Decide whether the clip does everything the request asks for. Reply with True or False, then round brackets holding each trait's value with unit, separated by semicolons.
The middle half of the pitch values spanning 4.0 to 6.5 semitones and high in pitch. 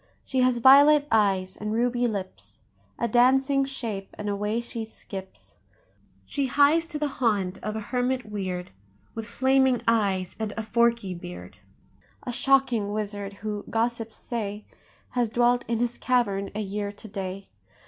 False (3.5 semitones; 225 Hz)